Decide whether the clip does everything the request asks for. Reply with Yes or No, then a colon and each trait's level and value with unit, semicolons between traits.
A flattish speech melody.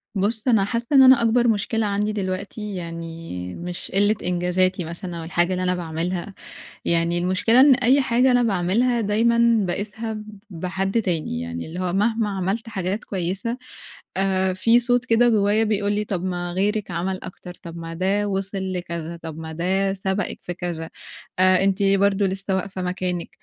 No: average, 3.4 semitones